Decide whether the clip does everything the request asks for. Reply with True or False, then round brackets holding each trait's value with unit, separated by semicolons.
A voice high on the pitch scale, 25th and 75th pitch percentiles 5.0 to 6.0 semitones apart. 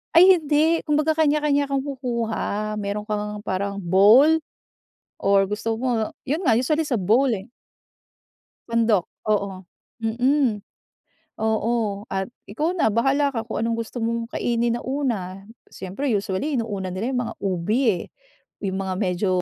True (230 Hz; 5.3 semitones)